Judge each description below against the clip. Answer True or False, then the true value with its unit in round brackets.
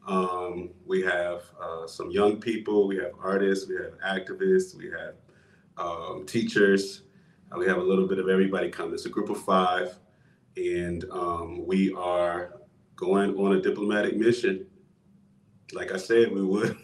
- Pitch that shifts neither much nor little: True (3.9 semitones)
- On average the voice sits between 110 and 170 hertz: False (95 Hz)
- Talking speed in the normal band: True (160 wpm)